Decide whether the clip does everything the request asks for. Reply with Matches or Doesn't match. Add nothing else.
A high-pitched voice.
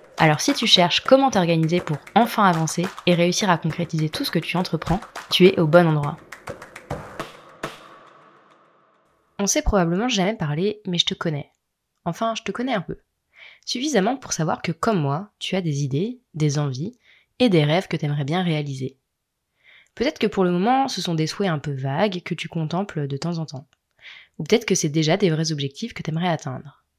Doesn't match